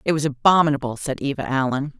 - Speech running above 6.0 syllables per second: Yes, 6.4 syllables/s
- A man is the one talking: No, female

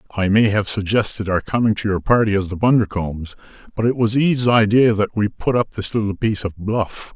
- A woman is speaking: No, male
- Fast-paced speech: Yes, fast, 220 wpm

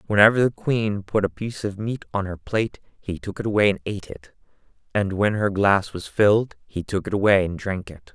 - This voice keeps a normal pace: No, fast, 230 wpm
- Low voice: Yes, low, 100 Hz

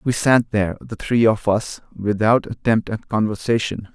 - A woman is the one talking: No, male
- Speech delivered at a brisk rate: No, average, 165 wpm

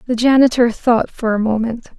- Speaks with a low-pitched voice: No, high, 235 Hz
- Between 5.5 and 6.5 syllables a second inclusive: No, 5.0 syllables/s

